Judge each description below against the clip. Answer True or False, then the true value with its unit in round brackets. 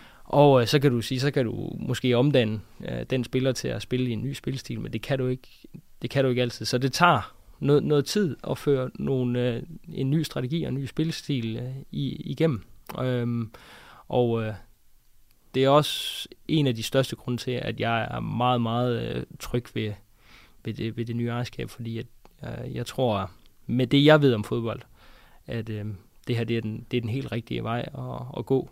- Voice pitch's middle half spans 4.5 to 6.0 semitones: False (2.9 semitones)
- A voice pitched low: True (125 Hz)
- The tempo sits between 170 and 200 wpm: False (215 wpm)